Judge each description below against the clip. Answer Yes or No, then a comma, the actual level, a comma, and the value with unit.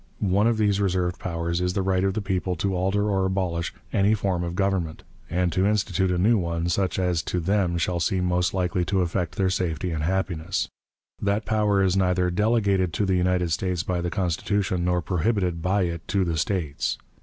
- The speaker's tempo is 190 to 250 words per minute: Yes, average, 200 wpm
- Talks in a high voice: No, very low, 90 Hz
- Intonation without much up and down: Yes, narrow, 2.0 semitones